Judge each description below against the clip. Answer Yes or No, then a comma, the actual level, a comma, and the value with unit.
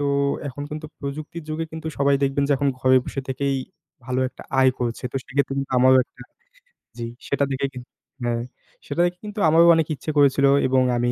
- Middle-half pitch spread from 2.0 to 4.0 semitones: Yes, average, 2.7 semitones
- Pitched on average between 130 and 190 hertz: Yes, medium, 140 Hz